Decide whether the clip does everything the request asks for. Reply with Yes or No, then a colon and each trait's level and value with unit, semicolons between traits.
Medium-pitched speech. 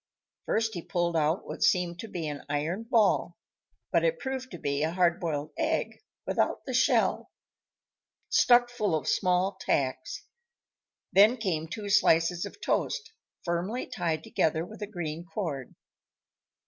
Yes: medium, 175 Hz